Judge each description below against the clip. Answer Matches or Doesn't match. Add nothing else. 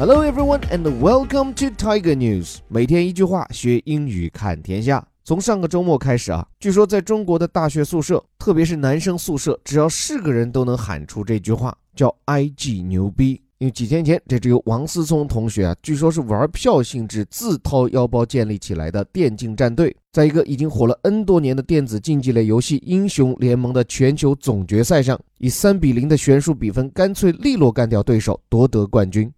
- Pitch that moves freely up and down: Matches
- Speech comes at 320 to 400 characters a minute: Matches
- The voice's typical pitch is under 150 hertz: Matches